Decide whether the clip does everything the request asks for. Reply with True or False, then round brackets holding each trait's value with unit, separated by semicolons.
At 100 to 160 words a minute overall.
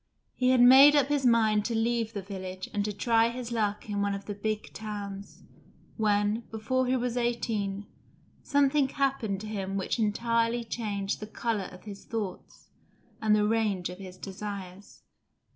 False (170 wpm)